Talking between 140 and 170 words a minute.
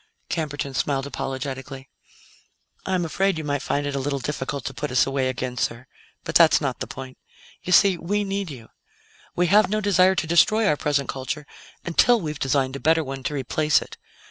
No: average, 195 wpm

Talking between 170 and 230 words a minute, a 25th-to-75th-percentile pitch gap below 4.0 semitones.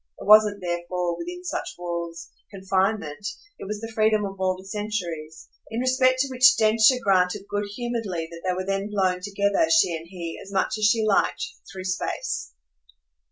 Yes: average, 175 wpm; average, 3.2 semitones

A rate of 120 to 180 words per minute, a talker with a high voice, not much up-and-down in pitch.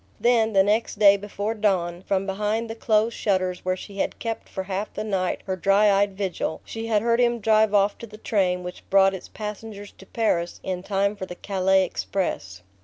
No: fast, 205 wpm; high, 200 Hz; narrow, 2.2 semitones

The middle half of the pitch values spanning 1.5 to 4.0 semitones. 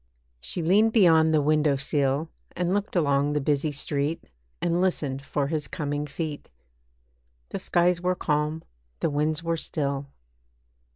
Yes: average, 2.8 semitones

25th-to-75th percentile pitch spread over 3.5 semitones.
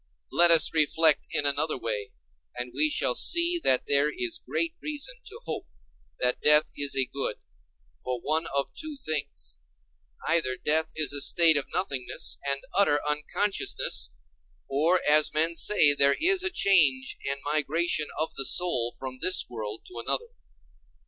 Yes: average, 4.3 semitones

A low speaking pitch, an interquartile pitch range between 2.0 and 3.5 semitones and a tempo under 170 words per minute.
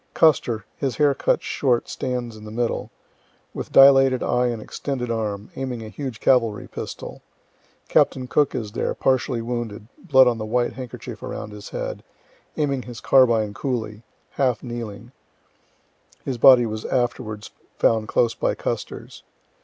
Yes: low, 120 Hz; average, 3.0 semitones; average, 145 wpm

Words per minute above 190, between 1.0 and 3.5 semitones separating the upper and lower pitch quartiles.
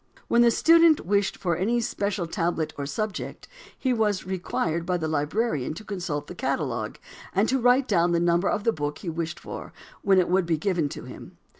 No: average, 200 wpm; average, 4.8 semitones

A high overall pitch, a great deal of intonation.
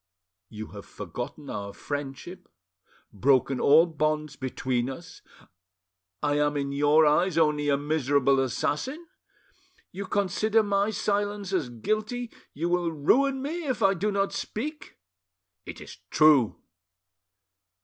No: medium, 155 Hz; wide, 6.4 semitones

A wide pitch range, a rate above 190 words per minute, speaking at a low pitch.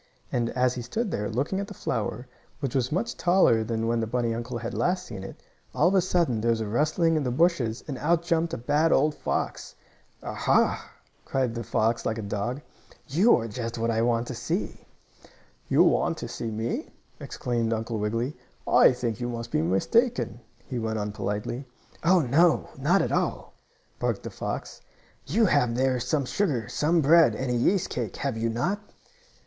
Yes: wide, 5.8 semitones; average, 200 wpm; low, 125 Hz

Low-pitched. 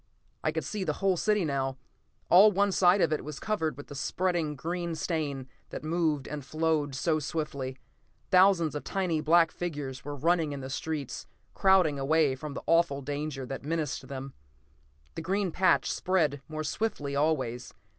No: medium, 155 Hz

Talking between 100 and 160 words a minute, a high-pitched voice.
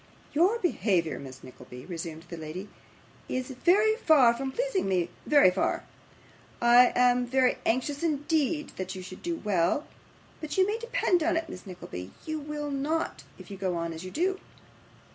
No: average, 170 wpm; very high, 255 Hz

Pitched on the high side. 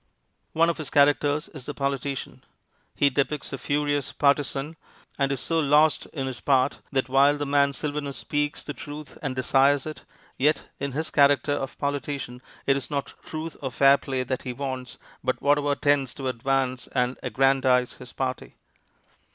No: medium, 140 Hz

